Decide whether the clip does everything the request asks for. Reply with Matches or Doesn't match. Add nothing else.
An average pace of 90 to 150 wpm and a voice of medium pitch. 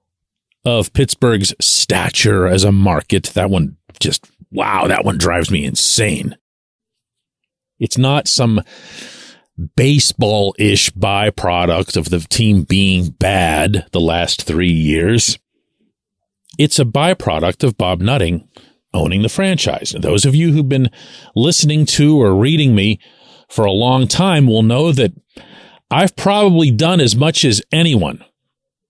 Doesn't match